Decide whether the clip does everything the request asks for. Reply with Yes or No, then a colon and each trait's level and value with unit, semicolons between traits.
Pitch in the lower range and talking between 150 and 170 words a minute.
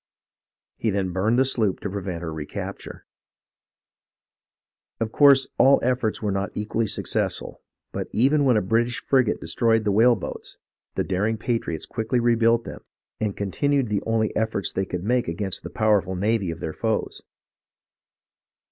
Yes: low, 110 Hz; average, 155 wpm